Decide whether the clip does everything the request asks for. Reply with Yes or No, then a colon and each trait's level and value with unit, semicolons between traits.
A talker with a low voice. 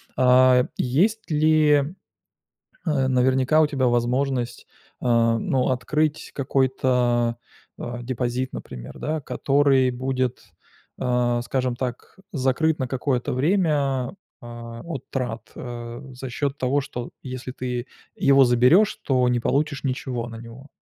Yes: low, 130 Hz